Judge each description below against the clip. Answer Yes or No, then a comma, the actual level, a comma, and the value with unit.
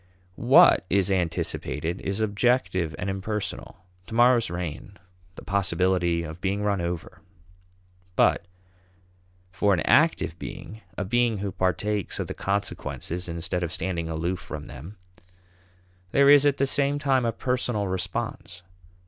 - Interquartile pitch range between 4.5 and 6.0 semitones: No, average, 4.0 semitones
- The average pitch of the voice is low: Yes, very low, 95 Hz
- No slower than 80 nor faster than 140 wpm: Yes, slow, 135 wpm